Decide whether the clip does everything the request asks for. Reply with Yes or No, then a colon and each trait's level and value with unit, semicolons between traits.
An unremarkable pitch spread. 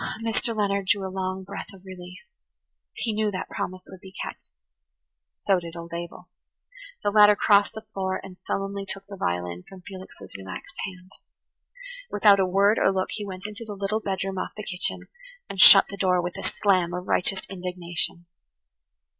No: narrow, 1.6 semitones